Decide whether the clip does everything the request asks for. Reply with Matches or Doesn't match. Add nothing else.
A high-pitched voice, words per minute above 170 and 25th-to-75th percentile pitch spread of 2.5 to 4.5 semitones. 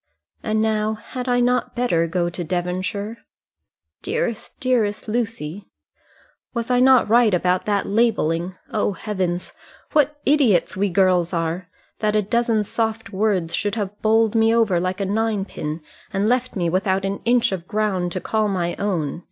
Doesn't match